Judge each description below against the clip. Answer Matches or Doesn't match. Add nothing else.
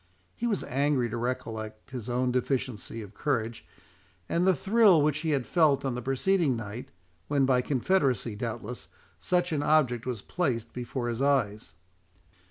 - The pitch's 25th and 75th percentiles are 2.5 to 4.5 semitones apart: Matches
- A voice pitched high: Doesn't match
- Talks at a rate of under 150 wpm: Doesn't match